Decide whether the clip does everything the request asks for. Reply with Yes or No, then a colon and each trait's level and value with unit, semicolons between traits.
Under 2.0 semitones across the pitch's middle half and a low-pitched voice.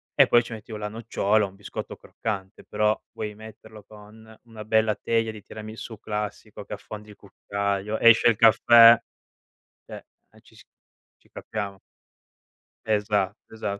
Yes: narrow, 1.3 semitones; low, 105 Hz